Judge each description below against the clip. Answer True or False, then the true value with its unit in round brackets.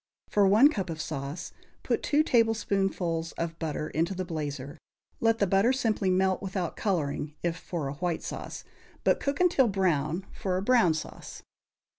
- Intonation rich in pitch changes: False (4.4 semitones)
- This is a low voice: False (185 Hz)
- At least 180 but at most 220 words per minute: False (165 wpm)